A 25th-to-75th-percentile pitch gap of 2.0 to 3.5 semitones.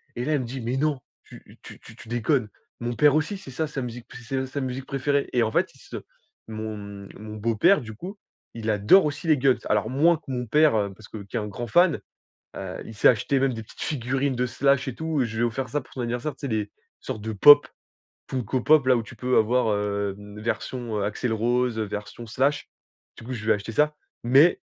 No: average, 4.1 semitones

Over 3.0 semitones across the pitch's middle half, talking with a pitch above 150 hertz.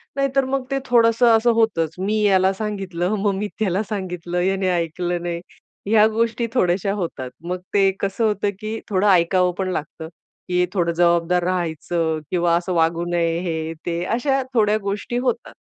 Yes: average, 3.8 semitones; medium, 185 Hz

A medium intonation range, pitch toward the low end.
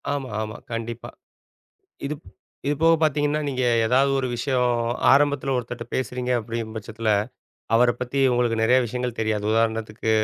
Yes: average, 3.1 semitones; low, 125 Hz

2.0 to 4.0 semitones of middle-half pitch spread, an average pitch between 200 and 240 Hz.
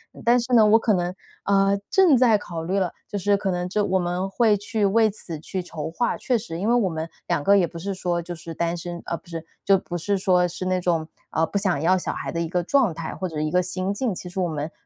No: average, 3.2 semitones; medium, 185 Hz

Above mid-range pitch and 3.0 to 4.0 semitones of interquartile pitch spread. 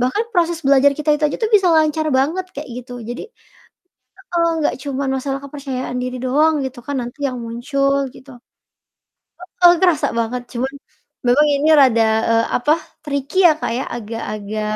Yes: very high, 275 Hz; average, 3.5 semitones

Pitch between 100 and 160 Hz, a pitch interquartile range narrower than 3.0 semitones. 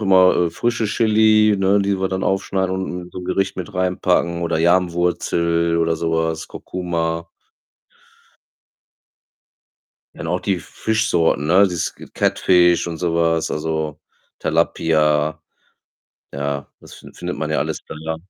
No: very low, 85 Hz; narrow, 2.5 semitones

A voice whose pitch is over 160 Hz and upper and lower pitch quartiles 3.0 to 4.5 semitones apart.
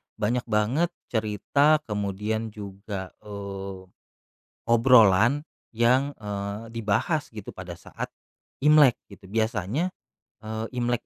No: low, 110 Hz; average, 3.4 semitones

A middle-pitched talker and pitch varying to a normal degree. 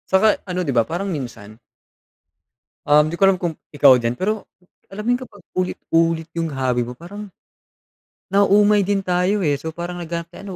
Yes: medium, 175 Hz; average, 4.8 semitones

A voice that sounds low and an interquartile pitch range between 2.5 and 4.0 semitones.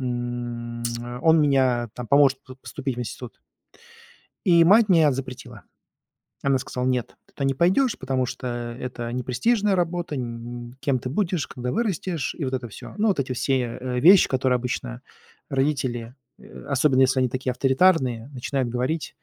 Yes: low, 130 Hz; average, 3.6 semitones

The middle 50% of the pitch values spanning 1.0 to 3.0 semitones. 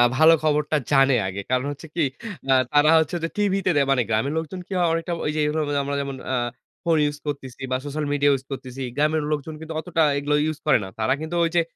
Yes: average, 2.7 semitones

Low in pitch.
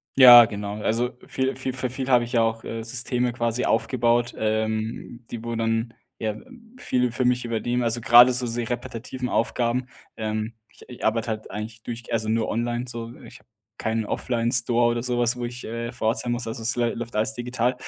Yes: low, 120 Hz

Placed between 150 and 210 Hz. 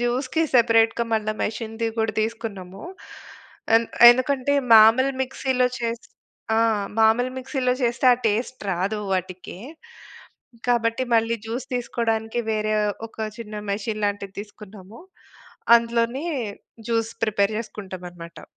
No: high, 225 Hz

